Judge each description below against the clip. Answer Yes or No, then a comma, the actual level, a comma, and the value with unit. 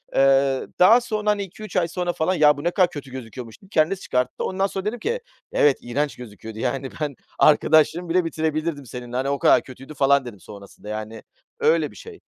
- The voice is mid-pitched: Yes, medium, 150 Hz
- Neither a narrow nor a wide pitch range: No, wide, 6.2 semitones